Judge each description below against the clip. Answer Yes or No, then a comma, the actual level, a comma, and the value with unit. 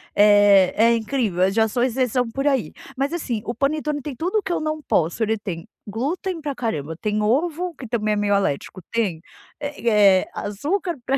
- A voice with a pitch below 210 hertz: No, high, 235 Hz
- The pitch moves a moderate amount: No, wide, 5.9 semitones